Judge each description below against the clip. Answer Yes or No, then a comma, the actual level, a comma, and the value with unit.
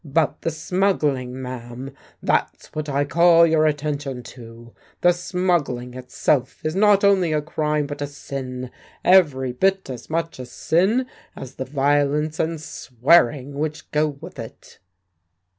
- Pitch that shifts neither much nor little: Yes, average, 4.1 semitones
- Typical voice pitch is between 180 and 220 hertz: No, medium, 145 Hz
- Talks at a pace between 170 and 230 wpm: No, average, 140 wpm